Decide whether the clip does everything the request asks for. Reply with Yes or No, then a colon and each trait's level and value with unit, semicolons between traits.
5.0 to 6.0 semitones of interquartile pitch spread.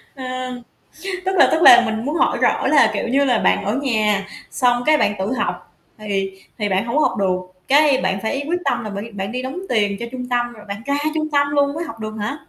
Yes: average, 5.3 semitones